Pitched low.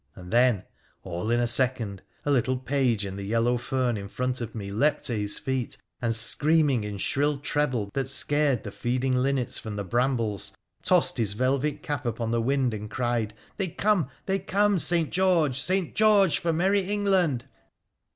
Yes: low, 130 Hz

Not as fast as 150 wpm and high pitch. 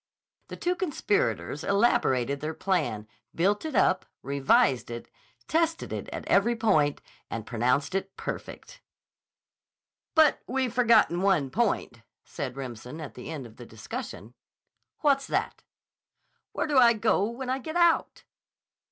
Yes: slow, 135 wpm; high, 195 Hz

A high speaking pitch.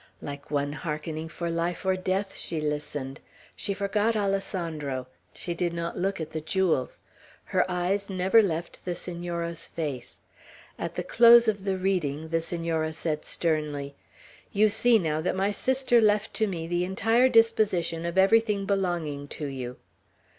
No: medium, 175 Hz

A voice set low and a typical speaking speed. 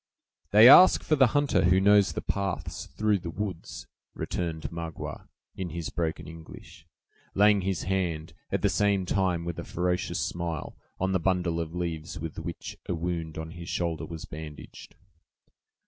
Yes: very low, 85 Hz; average, 165 wpm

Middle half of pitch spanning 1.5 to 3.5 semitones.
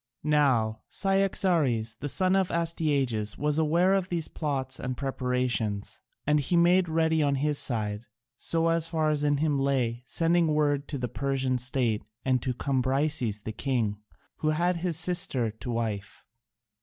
No: average, 4.8 semitones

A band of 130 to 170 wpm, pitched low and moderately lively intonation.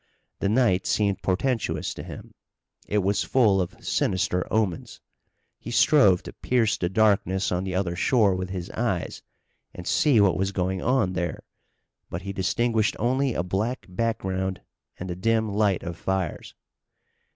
Yes: average, 155 wpm; very low, 95 Hz; average, 3.4 semitones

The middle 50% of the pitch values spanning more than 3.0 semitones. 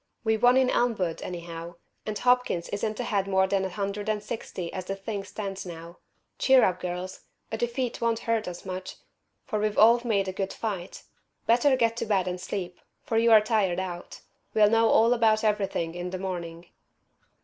Yes: average, 3.8 semitones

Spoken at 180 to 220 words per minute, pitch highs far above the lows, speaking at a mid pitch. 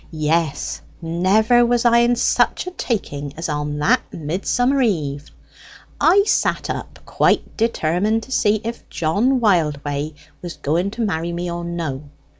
No: average, 145 wpm; wide, 6.9 semitones; medium, 175 Hz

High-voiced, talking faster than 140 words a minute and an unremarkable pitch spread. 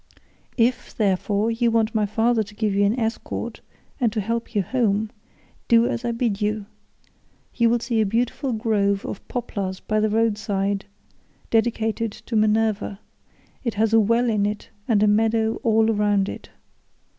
No: high, 220 Hz; average, 170 wpm; narrow, 1.8 semitones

